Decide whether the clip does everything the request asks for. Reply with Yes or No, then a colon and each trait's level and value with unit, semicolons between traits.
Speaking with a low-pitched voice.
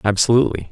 Yes: low, 110 Hz